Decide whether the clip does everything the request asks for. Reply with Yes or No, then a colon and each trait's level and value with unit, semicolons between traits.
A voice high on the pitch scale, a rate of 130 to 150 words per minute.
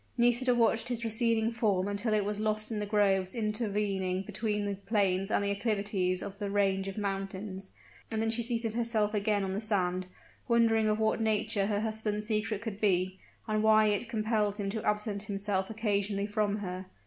No: high, 210 Hz; average, 185 wpm